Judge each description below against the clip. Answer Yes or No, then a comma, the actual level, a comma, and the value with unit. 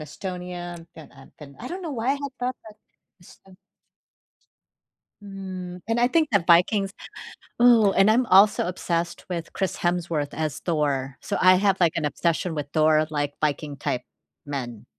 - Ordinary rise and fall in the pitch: Yes, average, 4.5 semitones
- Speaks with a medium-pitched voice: Yes, medium, 175 Hz